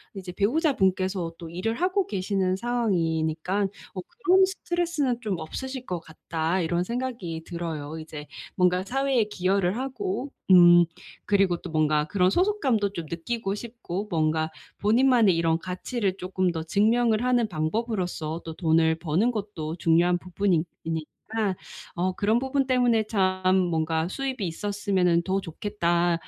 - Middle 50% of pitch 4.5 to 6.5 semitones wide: Yes, average, 5.3 semitones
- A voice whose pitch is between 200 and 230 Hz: No, medium, 185 Hz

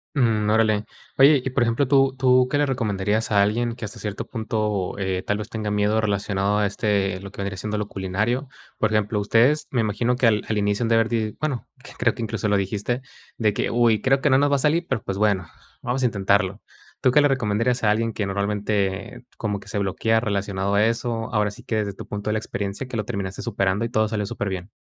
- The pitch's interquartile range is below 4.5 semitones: Yes, average, 2.9 semitones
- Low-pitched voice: Yes, low, 110 Hz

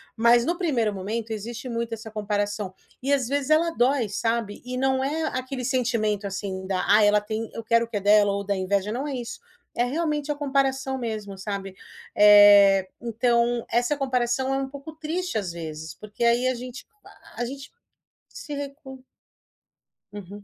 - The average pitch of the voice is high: Yes, high, 235 Hz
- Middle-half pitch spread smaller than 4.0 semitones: No, average, 4.4 semitones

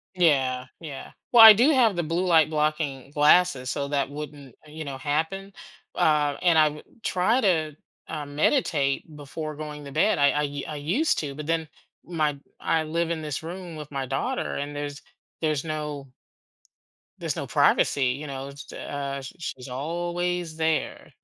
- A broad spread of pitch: No, average, 2.9 semitones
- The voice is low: No, medium, 150 Hz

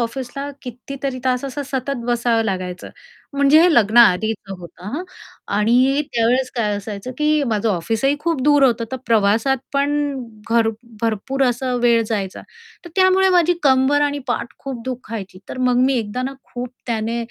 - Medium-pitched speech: No, high, 245 Hz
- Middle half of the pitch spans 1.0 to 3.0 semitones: No, average, 3.7 semitones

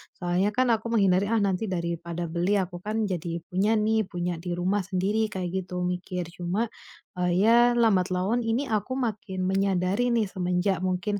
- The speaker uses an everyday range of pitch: Yes, average, 3.1 semitones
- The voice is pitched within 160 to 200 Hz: Yes, high, 190 Hz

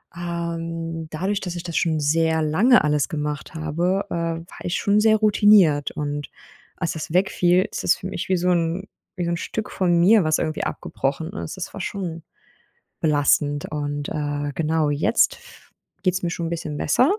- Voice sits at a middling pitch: Yes, medium, 165 Hz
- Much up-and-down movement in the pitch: No, average, 3.2 semitones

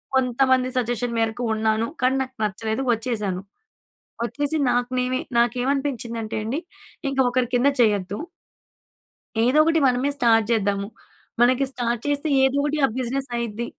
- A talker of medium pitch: No, high, 245 Hz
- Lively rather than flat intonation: No, average, 2.8 semitones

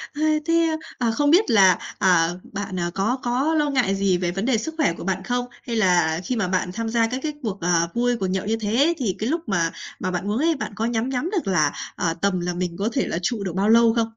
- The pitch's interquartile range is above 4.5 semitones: Yes, average, 5.2 semitones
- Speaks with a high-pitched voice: Yes, high, 215 Hz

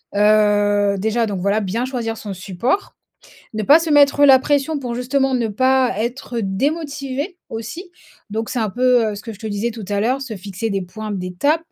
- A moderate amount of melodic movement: Yes, average, 4.5 semitones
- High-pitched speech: Yes, high, 230 Hz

